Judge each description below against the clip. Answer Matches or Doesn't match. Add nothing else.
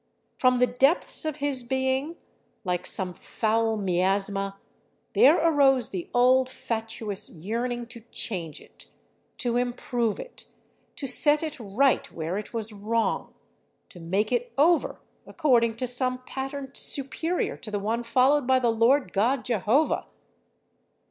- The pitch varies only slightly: Doesn't match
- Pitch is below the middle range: Doesn't match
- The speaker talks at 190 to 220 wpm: Doesn't match